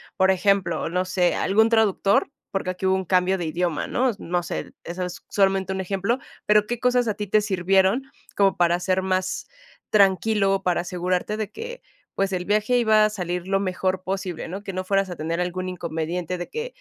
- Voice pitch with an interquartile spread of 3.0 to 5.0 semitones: No, narrow, 2.5 semitones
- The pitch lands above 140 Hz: Yes, high, 190 Hz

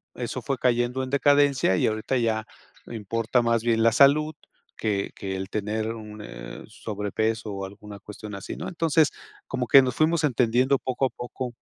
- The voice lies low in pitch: Yes, low, 115 Hz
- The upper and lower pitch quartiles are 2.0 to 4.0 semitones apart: Yes, average, 3.6 semitones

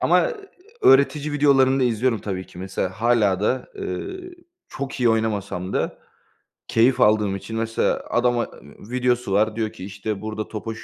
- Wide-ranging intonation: No, average, 3.9 semitones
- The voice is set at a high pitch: No, low, 115 Hz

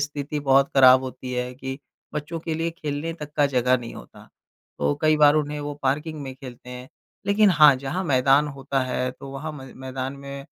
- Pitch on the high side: No, medium, 140 Hz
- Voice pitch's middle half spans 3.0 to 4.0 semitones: No, narrow, 2.4 semitones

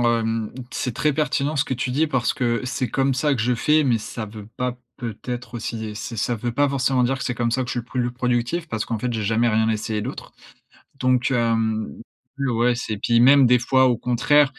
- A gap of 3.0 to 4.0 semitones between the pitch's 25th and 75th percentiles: No, narrow, 2.5 semitones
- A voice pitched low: Yes, low, 125 Hz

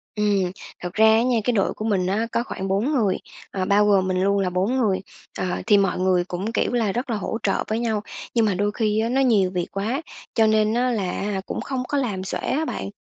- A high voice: Yes, high, 210 Hz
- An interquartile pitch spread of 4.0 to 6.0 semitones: No, average, 3.3 semitones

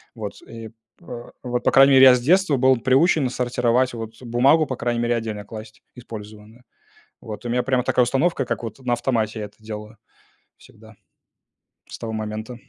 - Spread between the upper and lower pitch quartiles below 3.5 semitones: Yes, average, 2.8 semitones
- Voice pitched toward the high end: No, low, 120 Hz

